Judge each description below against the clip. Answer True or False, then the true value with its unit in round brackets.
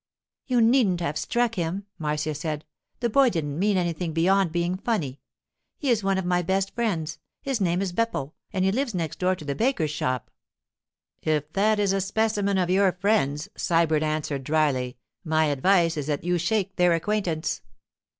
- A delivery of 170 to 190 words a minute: True (180 wpm)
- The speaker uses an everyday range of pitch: True (4.4 semitones)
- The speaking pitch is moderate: True (180 Hz)